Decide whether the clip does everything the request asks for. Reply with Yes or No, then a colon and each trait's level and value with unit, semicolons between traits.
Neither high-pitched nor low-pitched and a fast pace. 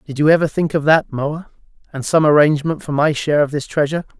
Yes: medium, 150 Hz; fast, 230 wpm